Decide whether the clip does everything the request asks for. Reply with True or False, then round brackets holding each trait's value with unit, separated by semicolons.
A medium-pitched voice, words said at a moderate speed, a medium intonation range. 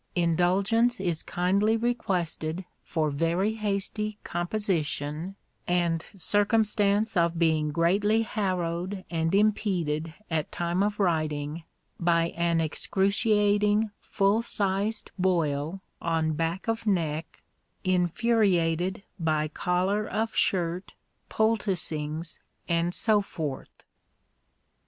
False (180 Hz; 95 wpm; 4.0 semitones)